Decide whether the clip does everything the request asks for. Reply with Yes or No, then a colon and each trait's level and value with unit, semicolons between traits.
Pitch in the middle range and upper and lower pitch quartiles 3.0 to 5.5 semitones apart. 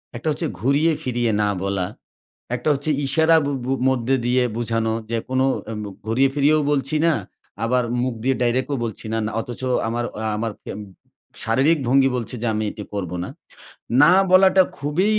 No: low, 130 Hz; average, 3.7 semitones